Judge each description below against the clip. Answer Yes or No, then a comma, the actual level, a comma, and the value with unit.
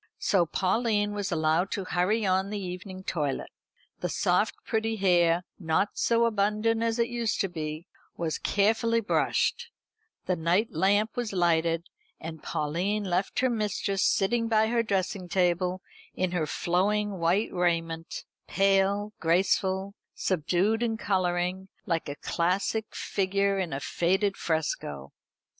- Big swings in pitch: No, average, 3.4 semitones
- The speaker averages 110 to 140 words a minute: Yes, slow, 135 wpm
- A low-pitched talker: No, high, 190 Hz